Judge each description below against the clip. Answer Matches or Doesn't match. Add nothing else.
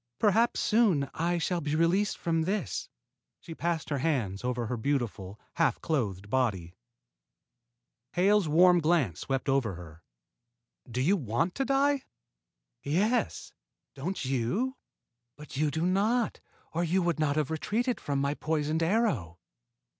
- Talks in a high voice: Doesn't match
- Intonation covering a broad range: Matches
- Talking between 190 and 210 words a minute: Doesn't match